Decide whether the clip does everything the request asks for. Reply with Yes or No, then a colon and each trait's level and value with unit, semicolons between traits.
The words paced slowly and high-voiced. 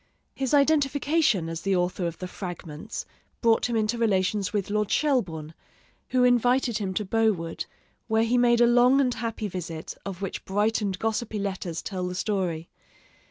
No: average, 165 wpm; high, 210 Hz